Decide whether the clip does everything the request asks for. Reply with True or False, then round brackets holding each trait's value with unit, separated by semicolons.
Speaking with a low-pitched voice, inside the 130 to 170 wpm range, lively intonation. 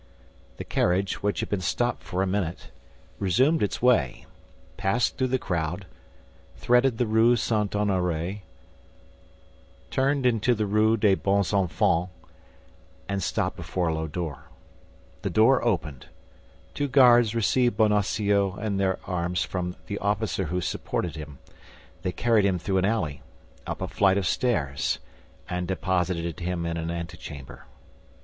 False (95 Hz; 140 wpm; 3.9 semitones)